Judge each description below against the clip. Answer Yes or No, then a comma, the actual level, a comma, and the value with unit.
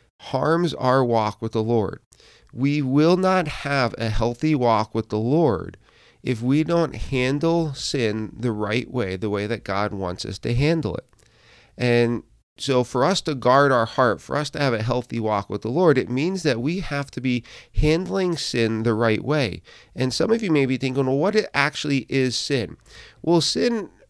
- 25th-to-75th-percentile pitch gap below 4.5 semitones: No, average, 4.8 semitones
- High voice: No, low, 130 Hz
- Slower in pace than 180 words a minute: No, average, 195 wpm